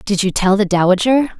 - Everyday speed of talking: No, fast, 215 wpm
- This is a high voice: Yes, high, 205 Hz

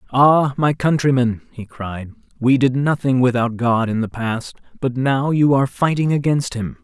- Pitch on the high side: No, low, 130 Hz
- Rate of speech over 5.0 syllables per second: No, 4.6 syllables/s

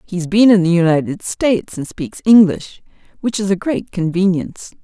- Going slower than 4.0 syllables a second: No, 5.2 syllables/s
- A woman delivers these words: Yes, female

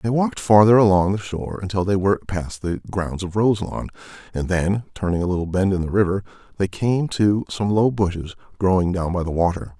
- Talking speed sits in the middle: No, fast, 210 wpm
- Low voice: Yes, very low, 95 Hz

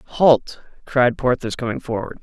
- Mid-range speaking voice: No, low, 130 Hz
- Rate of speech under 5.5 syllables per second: Yes, 4.1 syllables/s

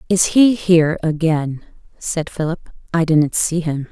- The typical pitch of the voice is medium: Yes, medium, 165 Hz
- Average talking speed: Yes, average, 155 wpm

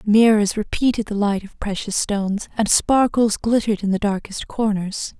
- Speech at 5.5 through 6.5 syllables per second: No, 4.8 syllables/s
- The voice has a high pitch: Yes, high, 210 Hz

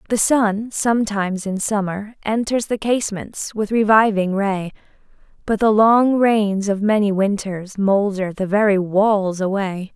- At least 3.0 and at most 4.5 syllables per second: Yes, 4.2 syllables/s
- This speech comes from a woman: Yes, female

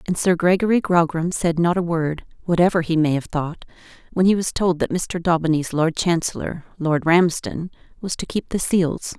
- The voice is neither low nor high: Yes, medium, 170 Hz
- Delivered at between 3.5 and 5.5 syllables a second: Yes, 4.9 syllables/s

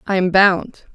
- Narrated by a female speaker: Yes, female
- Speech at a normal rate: Yes, average, 190 wpm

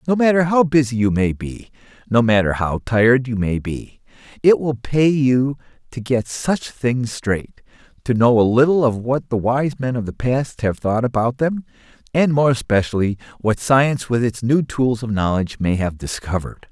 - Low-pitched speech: Yes, low, 120 Hz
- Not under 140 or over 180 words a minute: No, average, 190 wpm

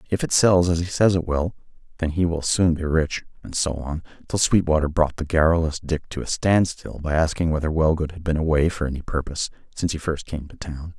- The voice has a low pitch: Yes, very low, 80 Hz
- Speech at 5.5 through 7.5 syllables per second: Yes, 5.7 syllables/s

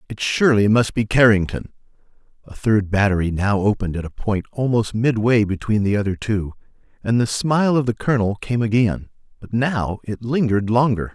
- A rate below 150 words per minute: No, average, 170 wpm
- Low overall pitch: Yes, low, 110 Hz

